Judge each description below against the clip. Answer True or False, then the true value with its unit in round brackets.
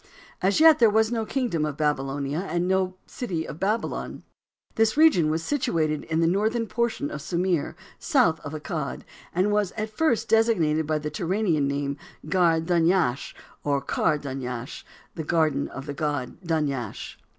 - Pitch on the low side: False (165 Hz)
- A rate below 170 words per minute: True (160 wpm)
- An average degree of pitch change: False (6.2 semitones)